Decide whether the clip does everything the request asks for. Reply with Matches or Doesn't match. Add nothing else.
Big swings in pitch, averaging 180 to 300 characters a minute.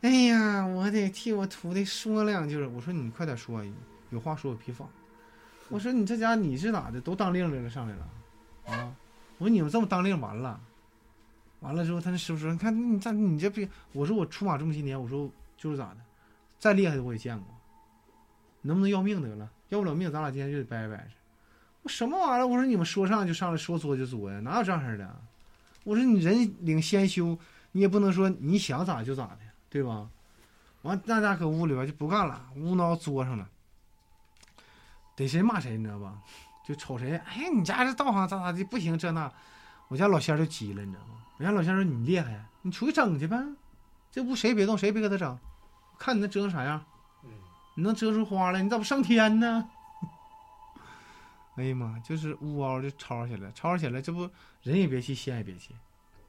Matches